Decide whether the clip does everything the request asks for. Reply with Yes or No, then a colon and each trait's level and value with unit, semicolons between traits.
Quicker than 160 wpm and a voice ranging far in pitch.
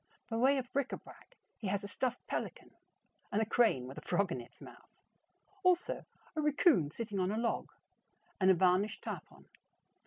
Yes: average, 185 wpm; wide, 5.8 semitones